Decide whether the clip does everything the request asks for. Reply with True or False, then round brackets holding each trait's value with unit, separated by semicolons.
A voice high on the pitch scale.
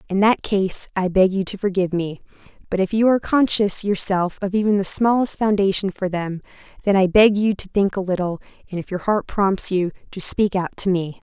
True (195 Hz)